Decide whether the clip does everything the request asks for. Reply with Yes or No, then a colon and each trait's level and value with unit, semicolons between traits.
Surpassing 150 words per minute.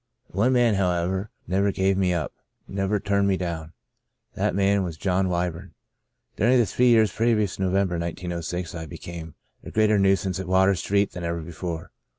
Yes: average, 180 wpm